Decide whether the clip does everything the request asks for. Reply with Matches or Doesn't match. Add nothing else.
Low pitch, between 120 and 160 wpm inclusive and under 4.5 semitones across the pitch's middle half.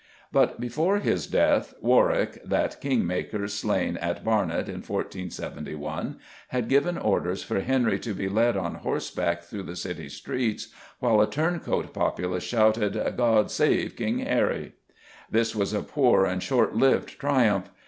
Doesn't match